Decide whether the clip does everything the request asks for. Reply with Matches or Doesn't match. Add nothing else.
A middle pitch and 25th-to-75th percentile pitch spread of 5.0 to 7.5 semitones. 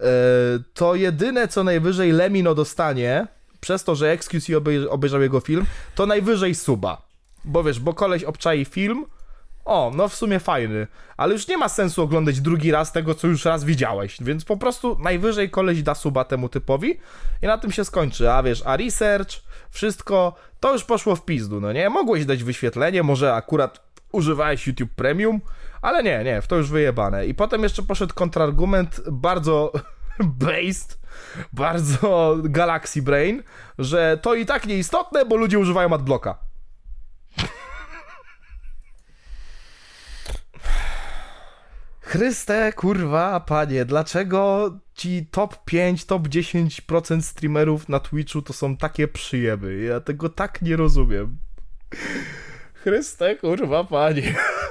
Matches